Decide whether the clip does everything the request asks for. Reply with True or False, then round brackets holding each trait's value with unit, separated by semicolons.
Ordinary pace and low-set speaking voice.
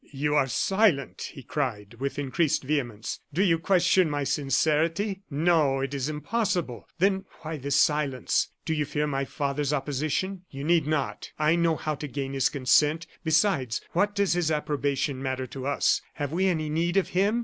False (175 wpm; 150 Hz)